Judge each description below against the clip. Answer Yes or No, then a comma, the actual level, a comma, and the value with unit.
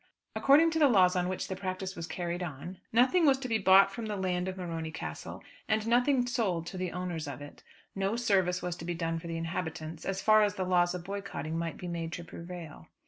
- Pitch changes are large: No, average, 3.3 semitones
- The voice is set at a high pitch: No, medium, 180 Hz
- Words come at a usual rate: No, fast, 235 wpm